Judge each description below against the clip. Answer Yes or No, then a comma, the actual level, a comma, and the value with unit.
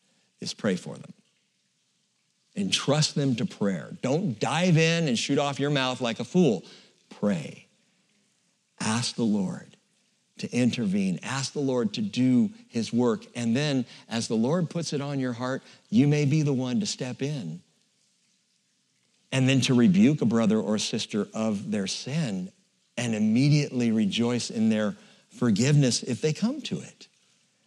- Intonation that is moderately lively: No, wide, 7.9 semitones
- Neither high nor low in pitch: Yes, medium, 145 Hz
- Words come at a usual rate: Yes, average, 155 wpm